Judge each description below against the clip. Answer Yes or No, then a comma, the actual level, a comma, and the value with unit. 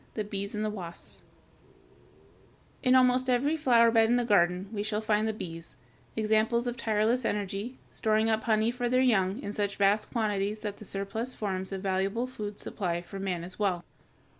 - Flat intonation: No, average, 3.0 semitones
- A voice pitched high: Yes, high, 215 Hz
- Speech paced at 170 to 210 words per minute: Yes, average, 180 wpm